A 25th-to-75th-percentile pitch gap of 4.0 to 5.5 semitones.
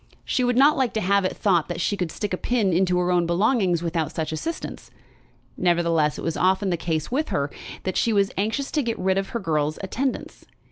Yes: average, 4.7 semitones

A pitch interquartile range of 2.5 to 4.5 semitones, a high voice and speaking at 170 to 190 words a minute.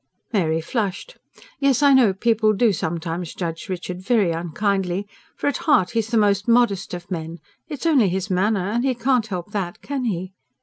No: average, 4.9 semitones; high, 200 Hz; average, 180 wpm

